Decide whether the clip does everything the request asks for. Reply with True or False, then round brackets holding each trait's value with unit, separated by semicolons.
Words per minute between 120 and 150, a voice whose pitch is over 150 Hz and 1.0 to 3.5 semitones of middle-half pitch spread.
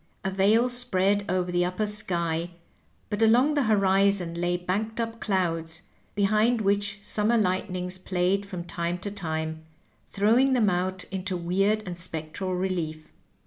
True (145 wpm; 190 Hz; 3.0 semitones)